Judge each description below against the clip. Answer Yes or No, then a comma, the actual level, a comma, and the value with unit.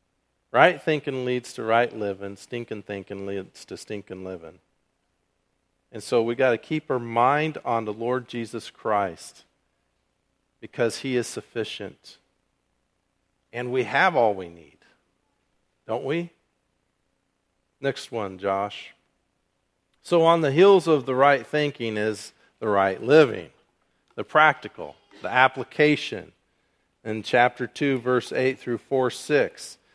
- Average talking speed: No, slow, 130 wpm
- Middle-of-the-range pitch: No, low, 115 Hz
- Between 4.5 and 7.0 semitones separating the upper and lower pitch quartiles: Yes, average, 5.0 semitones